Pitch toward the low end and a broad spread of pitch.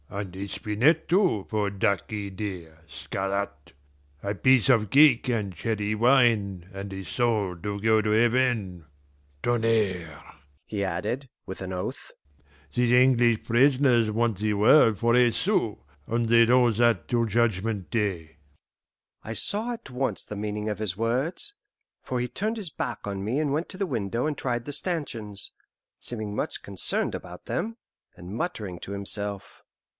No: low, 110 Hz; average, 3.7 semitones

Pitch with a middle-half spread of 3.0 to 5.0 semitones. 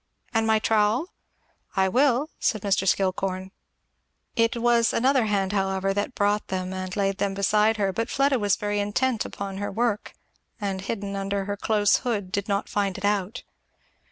No: narrow, 2.4 semitones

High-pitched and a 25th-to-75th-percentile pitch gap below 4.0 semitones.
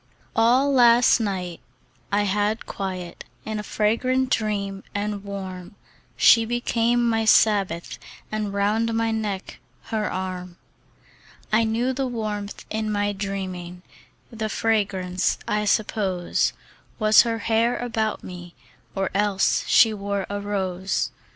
Yes: high, 210 Hz; narrow, 2.6 semitones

